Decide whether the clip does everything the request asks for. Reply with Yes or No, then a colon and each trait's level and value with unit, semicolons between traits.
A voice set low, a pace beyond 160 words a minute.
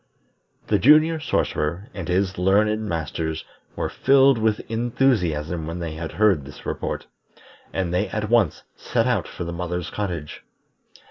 No: very low, 95 Hz; average, 140 wpm